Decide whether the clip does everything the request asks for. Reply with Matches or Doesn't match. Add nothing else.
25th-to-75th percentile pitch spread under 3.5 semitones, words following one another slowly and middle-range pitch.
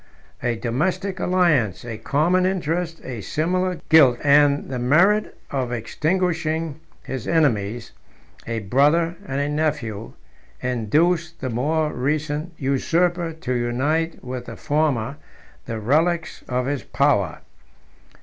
Doesn't match